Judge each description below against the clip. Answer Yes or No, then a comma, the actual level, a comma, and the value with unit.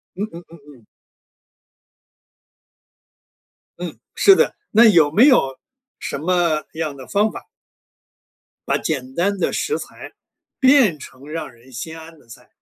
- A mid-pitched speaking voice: Yes, medium, 165 Hz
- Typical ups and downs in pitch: No, wide, 6.3 semitones